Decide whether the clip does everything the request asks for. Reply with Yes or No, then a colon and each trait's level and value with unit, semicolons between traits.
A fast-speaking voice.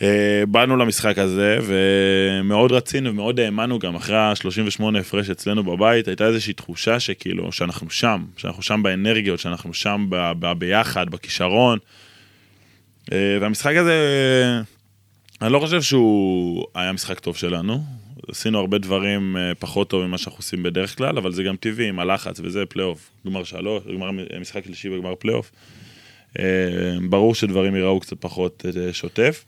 No: average, 140 wpm